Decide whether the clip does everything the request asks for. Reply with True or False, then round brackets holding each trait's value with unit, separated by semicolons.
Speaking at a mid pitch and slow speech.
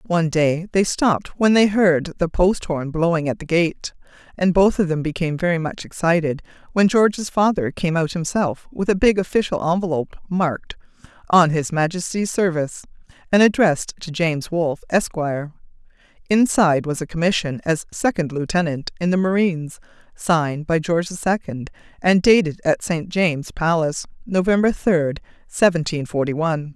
False (170 Hz; 155 wpm)